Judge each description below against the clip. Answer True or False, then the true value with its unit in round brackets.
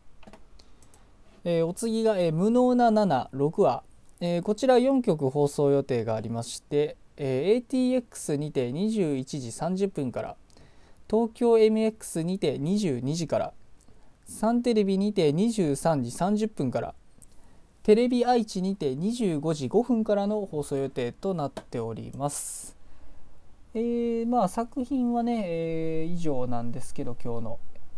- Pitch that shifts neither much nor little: False (8.5 semitones)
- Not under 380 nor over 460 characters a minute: False (215 characters per minute)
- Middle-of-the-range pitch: True (170 Hz)